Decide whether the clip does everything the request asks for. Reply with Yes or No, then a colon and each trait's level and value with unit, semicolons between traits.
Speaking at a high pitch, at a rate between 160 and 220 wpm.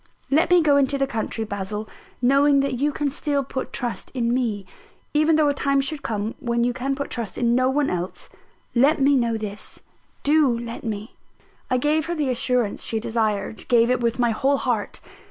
Yes: very high, 250 Hz; average, 200 wpm